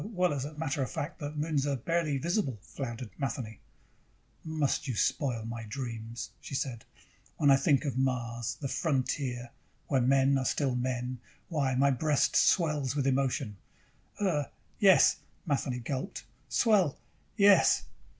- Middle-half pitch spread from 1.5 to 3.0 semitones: No, average, 3.4 semitones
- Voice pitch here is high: No, low, 135 Hz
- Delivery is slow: No, average, 150 wpm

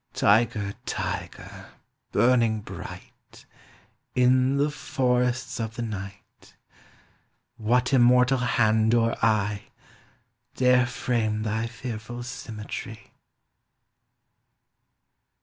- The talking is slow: Yes, slow, 80 wpm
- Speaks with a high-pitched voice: No, low, 120 Hz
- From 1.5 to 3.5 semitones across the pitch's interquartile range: Yes, narrow, 2.5 semitones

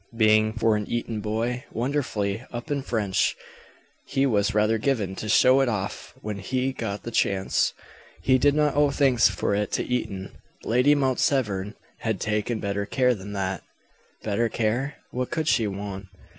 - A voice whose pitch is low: Yes, low, 110 Hz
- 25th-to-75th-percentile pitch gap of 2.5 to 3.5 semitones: No, average, 4.0 semitones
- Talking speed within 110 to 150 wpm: No, average, 170 wpm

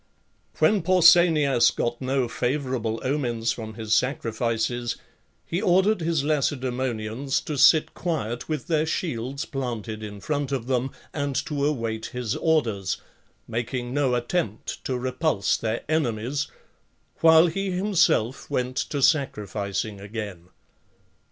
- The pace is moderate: No, slow, 120 wpm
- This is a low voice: Yes, low, 130 Hz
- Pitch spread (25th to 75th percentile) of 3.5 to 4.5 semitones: No, average, 5.0 semitones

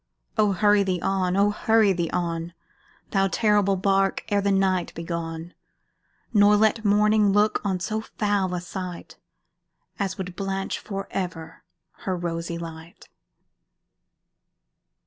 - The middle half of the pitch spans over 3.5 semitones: No, average, 2.8 semitones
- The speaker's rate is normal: No, slow, 130 wpm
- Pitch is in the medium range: No, high, 195 Hz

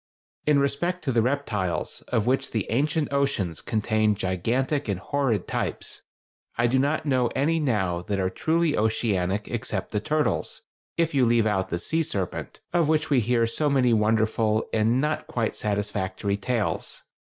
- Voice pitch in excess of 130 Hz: No, low, 115 Hz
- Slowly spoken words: No, average, 165 wpm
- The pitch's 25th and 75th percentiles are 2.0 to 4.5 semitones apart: No, average, 5.3 semitones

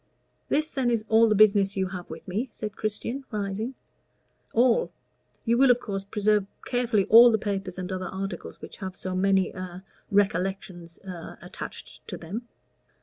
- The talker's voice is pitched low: No, high, 200 Hz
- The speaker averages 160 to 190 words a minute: Yes, average, 165 wpm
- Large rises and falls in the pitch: No, average, 3.3 semitones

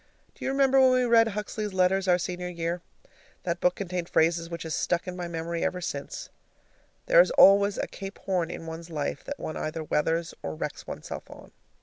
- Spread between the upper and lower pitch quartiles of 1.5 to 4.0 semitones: Yes, average, 3.3 semitones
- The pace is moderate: No, fast, 210 wpm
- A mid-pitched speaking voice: Yes, medium, 180 Hz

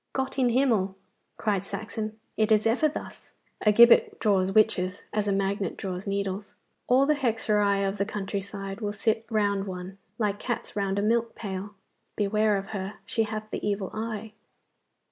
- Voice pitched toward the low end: No, high, 210 Hz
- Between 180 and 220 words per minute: No, average, 170 wpm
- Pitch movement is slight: Yes, narrow, 2.0 semitones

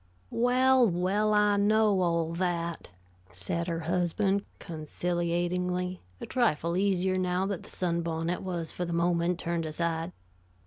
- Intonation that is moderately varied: No, narrow, 2.3 semitones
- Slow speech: Yes, slow, 130 wpm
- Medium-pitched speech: Yes, medium, 180 Hz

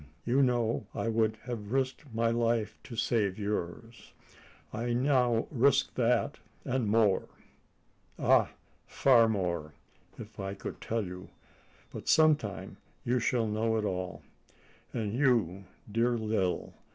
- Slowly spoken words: Yes, slow, 125 wpm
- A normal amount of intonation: Yes, average, 3.0 semitones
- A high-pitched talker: No, low, 115 Hz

